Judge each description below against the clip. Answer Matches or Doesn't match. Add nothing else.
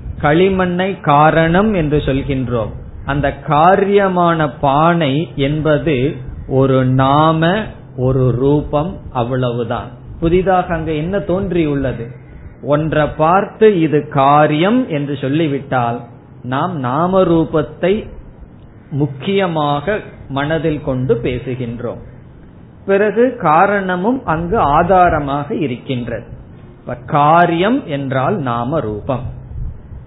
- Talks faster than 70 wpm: Matches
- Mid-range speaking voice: Matches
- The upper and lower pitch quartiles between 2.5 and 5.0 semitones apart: Matches